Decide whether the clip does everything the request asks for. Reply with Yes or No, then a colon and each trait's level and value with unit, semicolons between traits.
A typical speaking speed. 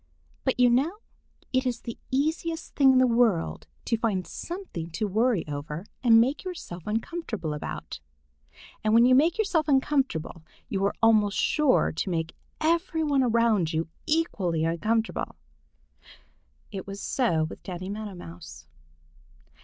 Yes: average, 145 wpm